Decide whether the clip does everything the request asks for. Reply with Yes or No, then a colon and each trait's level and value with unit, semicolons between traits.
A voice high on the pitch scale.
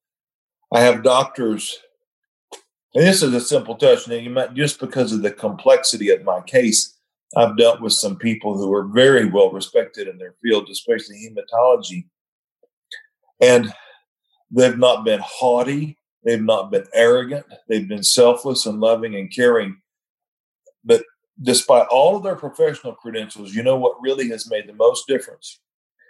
No: medium, 140 Hz